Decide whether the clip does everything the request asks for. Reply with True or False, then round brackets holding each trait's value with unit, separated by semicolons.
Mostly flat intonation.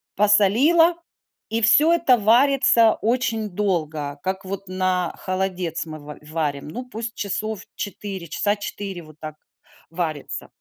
False (4.9 semitones)